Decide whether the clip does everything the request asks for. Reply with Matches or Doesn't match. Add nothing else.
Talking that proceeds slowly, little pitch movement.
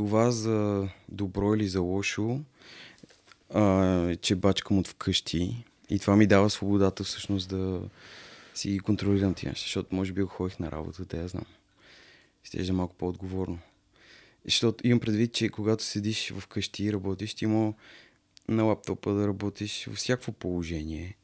Doesn't match